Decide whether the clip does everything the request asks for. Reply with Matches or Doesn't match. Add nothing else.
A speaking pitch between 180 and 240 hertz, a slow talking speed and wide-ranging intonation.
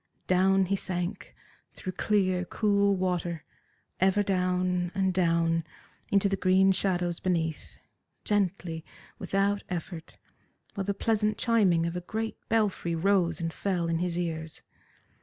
Doesn't match